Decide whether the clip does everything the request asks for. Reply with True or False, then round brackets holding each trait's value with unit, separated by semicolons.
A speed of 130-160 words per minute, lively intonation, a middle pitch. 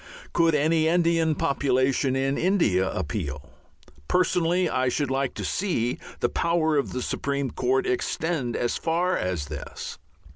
False (140 wpm; 5.0 semitones; 145 Hz)